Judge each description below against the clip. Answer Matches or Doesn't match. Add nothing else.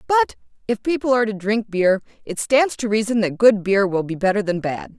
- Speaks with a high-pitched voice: Matches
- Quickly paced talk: Matches